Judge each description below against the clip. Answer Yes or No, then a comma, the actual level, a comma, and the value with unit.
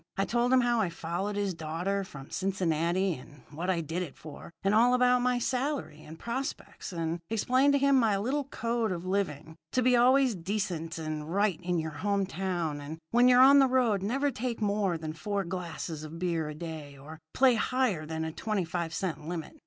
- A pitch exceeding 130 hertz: Yes, high, 190 Hz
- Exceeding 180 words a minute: Yes, fast, 205 wpm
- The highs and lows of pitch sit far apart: Yes, wide, 6.8 semitones